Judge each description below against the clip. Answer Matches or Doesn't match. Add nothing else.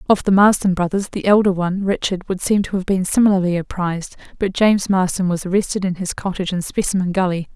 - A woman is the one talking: Matches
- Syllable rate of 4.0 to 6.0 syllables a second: Doesn't match